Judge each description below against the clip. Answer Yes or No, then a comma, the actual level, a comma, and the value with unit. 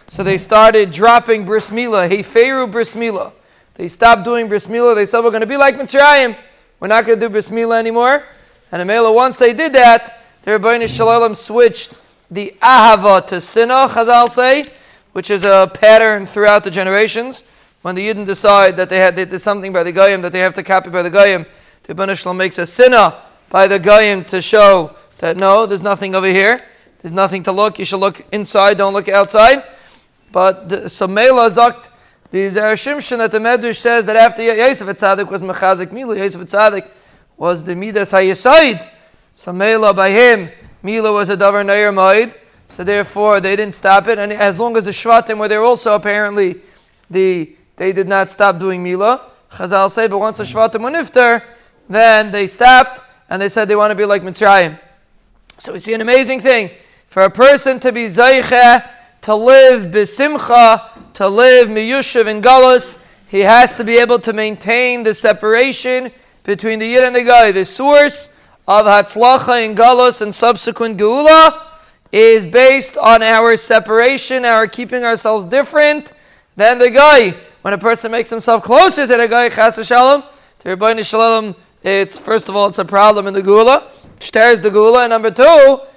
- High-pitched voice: Yes, high, 220 Hz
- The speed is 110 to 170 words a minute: No, average, 180 wpm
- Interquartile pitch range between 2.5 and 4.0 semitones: Yes, average, 3.4 semitones